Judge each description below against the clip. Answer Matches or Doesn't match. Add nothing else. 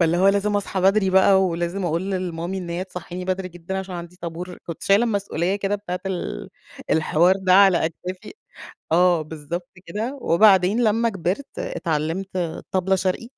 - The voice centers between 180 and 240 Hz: Matches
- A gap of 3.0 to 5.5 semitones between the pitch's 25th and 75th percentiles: Doesn't match